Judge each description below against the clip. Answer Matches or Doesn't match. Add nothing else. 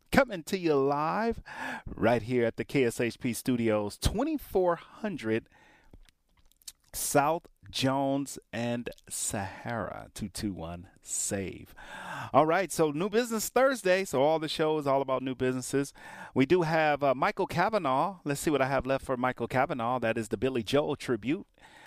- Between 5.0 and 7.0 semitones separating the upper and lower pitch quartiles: Matches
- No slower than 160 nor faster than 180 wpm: Doesn't match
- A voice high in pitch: Doesn't match